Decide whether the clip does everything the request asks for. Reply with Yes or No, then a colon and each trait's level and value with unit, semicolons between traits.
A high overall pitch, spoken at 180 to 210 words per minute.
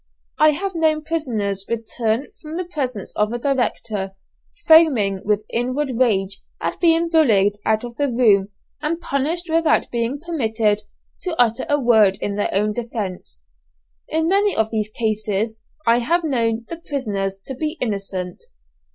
No: high, 235 Hz; average, 150 wpm